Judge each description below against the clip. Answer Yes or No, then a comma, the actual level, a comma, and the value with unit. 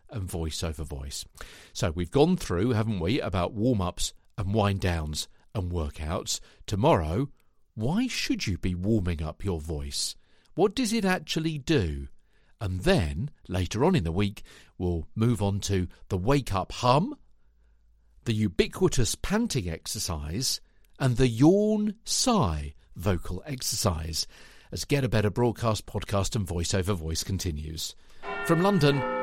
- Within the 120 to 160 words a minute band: Yes, average, 145 wpm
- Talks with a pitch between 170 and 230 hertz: No, low, 100 Hz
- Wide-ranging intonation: Yes, wide, 7.3 semitones